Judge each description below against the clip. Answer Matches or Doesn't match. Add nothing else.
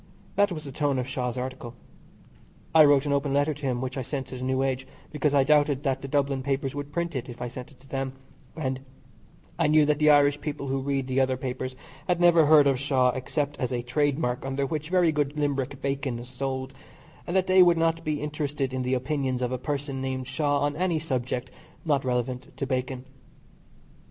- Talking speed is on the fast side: Matches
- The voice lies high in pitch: Doesn't match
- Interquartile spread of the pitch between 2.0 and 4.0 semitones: Matches